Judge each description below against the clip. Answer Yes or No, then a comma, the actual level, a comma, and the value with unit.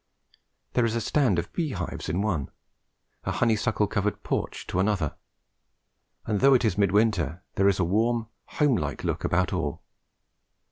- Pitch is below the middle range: Yes, low, 105 Hz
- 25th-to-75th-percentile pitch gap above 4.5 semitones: No, average, 4.2 semitones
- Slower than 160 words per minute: No, average, 170 wpm